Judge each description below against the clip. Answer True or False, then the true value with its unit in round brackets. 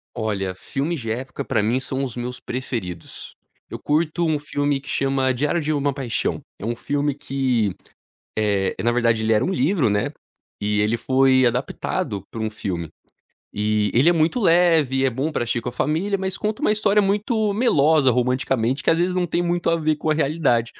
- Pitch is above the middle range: False (135 Hz)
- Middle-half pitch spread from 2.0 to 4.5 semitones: False (5.6 semitones)